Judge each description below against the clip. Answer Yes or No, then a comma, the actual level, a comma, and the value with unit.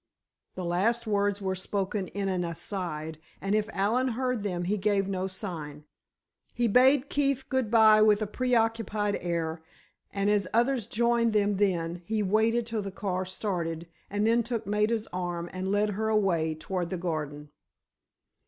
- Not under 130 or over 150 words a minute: No, average, 160 wpm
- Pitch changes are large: No, average, 3.6 semitones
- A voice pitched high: Yes, high, 200 Hz